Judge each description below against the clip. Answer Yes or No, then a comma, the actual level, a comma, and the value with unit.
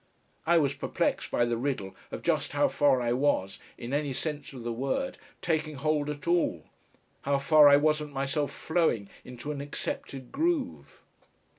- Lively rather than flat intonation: No, average, 3.1 semitones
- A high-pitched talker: No, medium, 145 Hz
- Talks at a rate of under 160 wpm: No, average, 165 wpm